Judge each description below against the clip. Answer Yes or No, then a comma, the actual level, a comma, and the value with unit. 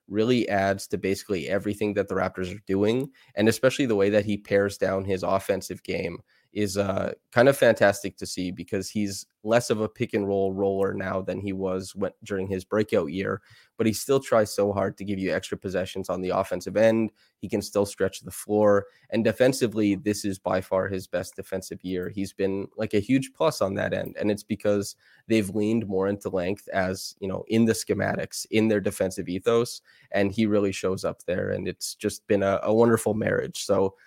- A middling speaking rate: No, fast, 210 wpm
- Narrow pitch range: Yes, narrow, 1.9 semitones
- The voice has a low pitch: Yes, low, 100 Hz